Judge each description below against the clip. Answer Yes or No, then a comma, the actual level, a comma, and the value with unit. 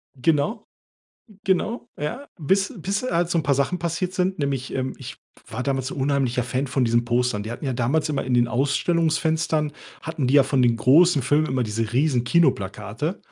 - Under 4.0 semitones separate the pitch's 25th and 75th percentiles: No, average, 4.9 semitones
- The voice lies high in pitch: No, medium, 140 Hz